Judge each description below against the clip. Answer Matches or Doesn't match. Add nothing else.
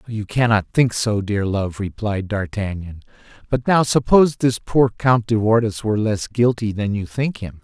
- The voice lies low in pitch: Matches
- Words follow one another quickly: Doesn't match